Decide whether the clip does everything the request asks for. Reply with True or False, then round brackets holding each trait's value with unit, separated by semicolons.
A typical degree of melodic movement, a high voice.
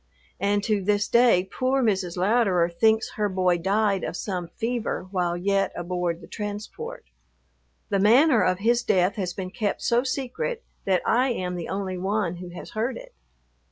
True (4.0 semitones; 200 Hz)